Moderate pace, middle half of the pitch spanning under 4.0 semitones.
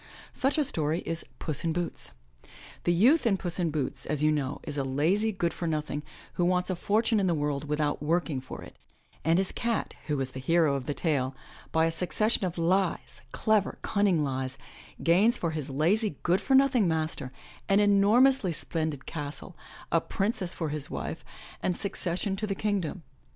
No: average, 190 wpm; average, 4.9 semitones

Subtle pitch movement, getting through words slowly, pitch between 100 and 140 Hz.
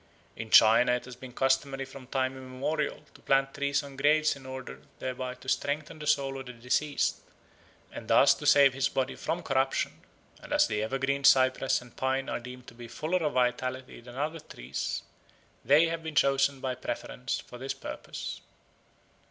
No: narrow, 2.0 semitones; average, 180 wpm; low, 135 Hz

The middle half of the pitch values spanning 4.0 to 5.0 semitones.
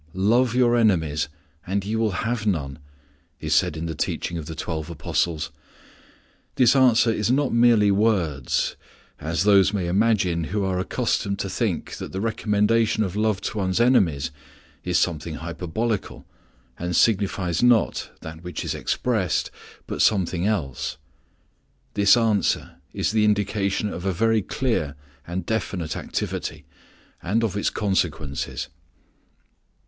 Yes: average, 4.6 semitones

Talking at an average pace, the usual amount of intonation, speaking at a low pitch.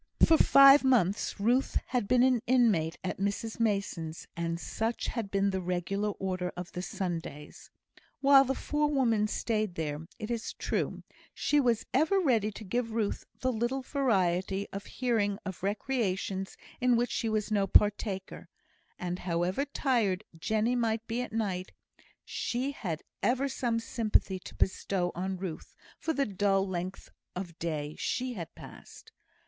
No: average, 155 wpm; average, 4.8 semitones; high, 210 Hz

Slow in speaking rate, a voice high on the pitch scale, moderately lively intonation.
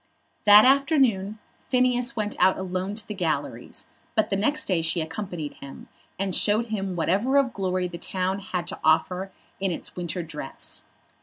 No: average, 165 wpm; high, 195 Hz; average, 3.4 semitones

